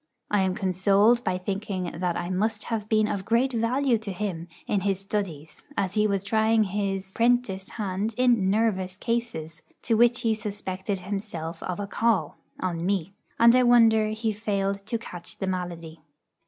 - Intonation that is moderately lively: Yes, average, 3.1 semitones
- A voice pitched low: No, high, 200 Hz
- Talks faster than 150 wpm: Yes, average, 170 wpm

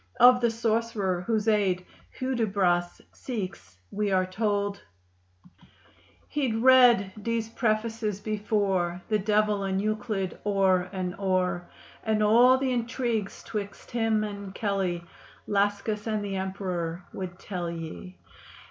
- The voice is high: Yes, high, 205 Hz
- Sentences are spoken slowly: Yes, slow, 120 wpm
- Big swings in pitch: No, average, 3.0 semitones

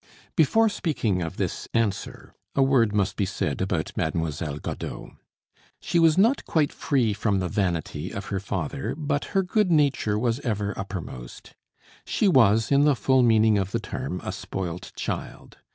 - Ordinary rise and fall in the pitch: No, wide, 7.0 semitones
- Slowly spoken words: No, average, 165 wpm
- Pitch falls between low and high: No, low, 110 Hz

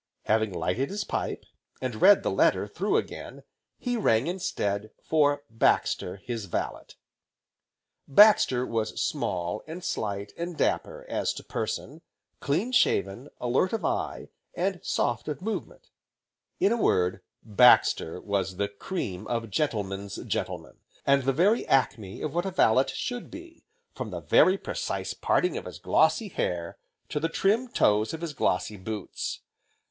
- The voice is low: Yes, low, 130 Hz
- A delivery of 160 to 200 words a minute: No, average, 145 wpm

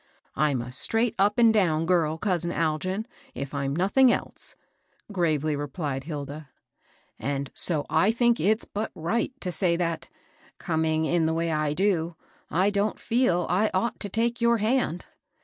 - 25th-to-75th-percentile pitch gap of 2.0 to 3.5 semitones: No, average, 5.2 semitones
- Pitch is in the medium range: Yes, medium, 175 Hz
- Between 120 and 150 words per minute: No, average, 165 wpm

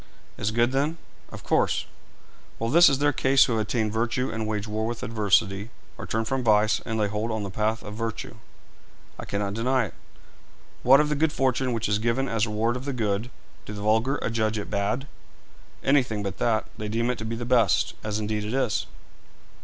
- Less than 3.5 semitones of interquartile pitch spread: Yes, average, 2.9 semitones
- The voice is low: Yes, low, 115 Hz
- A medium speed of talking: No, fast, 210 wpm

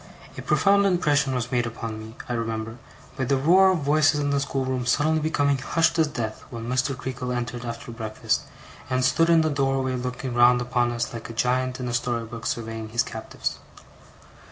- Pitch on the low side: Yes, low, 125 Hz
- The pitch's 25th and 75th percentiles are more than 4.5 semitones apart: No, average, 3.2 semitones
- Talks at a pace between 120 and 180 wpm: No, average, 195 wpm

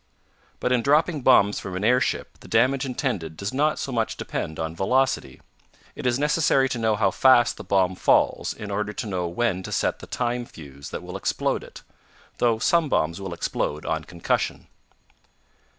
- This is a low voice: Yes, low, 110 Hz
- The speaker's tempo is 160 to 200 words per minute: Yes, average, 180 wpm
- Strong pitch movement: Yes, wide, 6.1 semitones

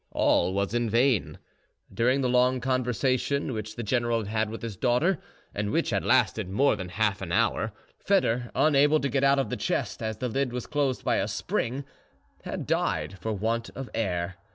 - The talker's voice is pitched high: No, low, 120 Hz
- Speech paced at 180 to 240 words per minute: Yes, average, 195 wpm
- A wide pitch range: No, average, 3.7 semitones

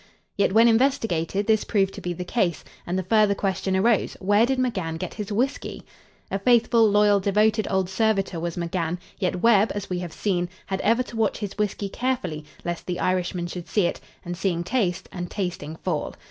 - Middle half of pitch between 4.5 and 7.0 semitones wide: No, average, 3.6 semitones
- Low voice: No, high, 195 Hz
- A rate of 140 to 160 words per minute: No, average, 195 wpm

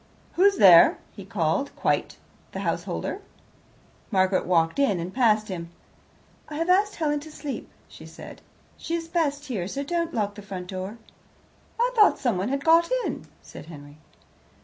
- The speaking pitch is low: No, high, 235 Hz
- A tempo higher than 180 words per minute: No, average, 160 wpm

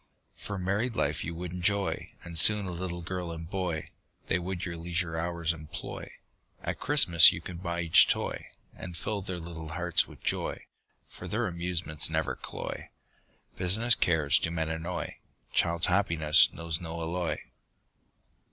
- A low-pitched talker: Yes, very low, 85 Hz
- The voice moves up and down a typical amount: No, narrow, 1.9 semitones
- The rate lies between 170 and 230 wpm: No, average, 155 wpm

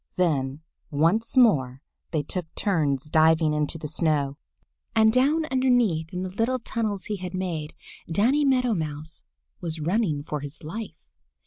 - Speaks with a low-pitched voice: No, medium, 170 Hz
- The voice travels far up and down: Yes, wide, 6.6 semitones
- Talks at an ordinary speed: Yes, average, 145 wpm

